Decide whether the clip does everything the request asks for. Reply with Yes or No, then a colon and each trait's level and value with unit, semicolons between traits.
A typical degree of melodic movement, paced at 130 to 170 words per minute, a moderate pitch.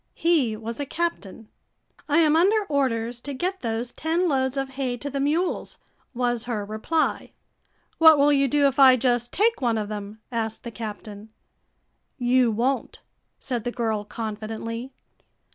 No: average, 4.2 semitones; average, 160 wpm; very high, 250 Hz